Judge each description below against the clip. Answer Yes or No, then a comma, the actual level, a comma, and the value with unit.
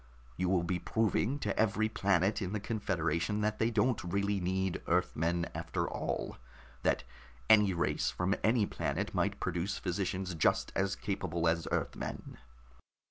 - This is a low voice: Yes, very low, 95 Hz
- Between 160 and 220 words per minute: No, average, 145 wpm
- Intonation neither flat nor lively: Yes, average, 3.2 semitones